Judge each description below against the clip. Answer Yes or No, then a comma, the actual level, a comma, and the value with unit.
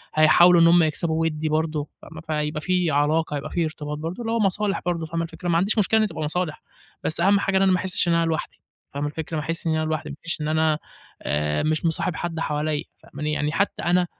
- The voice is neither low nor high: Yes, medium, 160 Hz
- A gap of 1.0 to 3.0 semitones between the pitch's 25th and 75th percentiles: Yes, narrow, 2.4 semitones